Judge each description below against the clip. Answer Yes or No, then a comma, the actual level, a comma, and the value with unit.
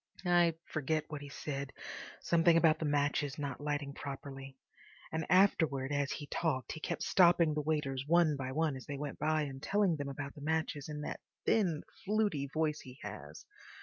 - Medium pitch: Yes, medium, 150 Hz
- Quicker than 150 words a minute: Yes, average, 180 wpm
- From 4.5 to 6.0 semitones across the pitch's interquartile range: No, narrow, 2.5 semitones